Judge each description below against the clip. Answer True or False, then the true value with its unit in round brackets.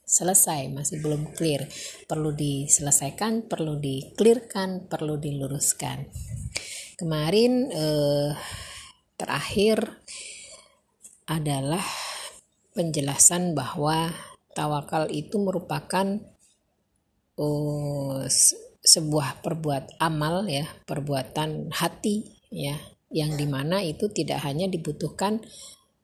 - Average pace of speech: False (75 wpm)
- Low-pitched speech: False (155 Hz)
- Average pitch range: True (4.2 semitones)